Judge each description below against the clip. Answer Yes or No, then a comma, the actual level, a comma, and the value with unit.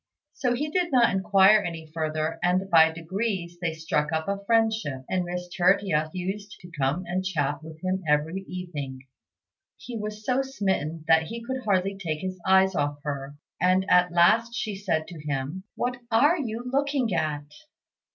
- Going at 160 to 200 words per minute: Yes, average, 170 wpm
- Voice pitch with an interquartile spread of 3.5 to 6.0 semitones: Yes, average, 4.9 semitones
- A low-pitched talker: No, medium, 185 Hz